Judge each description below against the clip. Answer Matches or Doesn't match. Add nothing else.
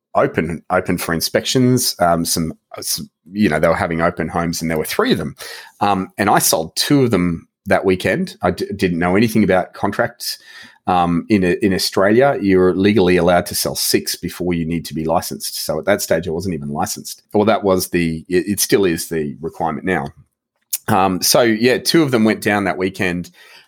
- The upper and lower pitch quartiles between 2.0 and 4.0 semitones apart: Matches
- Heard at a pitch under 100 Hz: Matches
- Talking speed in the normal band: Doesn't match